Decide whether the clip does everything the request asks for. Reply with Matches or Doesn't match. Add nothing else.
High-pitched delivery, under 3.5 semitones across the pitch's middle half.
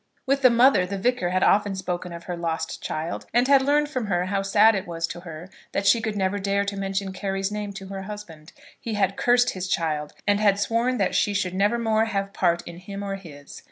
Matches